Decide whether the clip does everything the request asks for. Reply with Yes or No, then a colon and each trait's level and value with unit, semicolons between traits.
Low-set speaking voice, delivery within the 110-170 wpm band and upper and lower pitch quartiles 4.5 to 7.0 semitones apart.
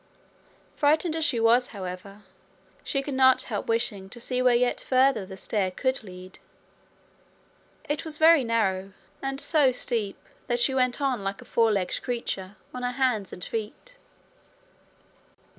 No: high, 240 Hz; average, 155 wpm; average, 4.9 semitones